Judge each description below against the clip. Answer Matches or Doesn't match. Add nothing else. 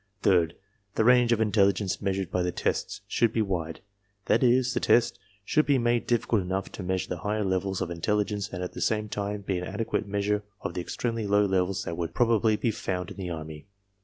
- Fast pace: Matches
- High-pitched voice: Doesn't match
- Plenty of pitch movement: Doesn't match